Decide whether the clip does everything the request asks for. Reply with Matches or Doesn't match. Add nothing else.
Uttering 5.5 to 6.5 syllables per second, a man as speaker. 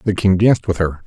Matches